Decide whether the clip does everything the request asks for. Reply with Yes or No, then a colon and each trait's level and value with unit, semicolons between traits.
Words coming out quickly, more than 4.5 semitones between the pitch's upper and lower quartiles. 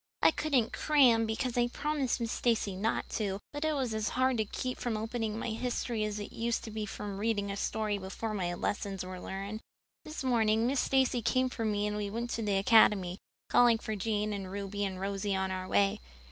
No: fast, 220 wpm; average, 3.1 semitones